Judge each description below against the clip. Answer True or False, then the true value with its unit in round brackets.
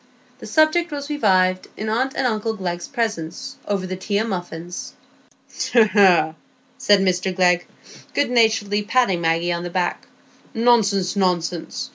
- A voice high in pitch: True (200 Hz)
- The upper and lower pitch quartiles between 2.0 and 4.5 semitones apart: True (4.2 semitones)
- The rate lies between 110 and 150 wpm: True (145 wpm)